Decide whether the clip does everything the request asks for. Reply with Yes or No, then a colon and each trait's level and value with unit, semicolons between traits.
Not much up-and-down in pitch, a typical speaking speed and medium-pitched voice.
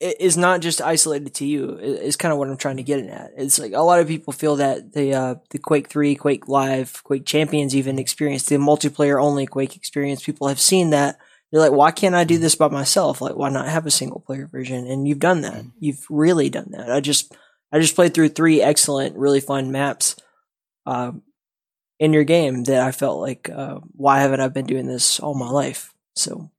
No: narrow, 2.1 semitones; fast, 220 wpm; medium, 145 Hz